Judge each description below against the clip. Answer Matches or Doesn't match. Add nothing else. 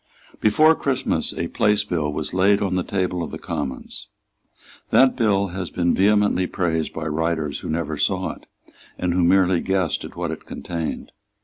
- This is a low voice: Matches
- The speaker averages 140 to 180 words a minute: Matches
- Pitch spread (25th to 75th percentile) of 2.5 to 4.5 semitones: Matches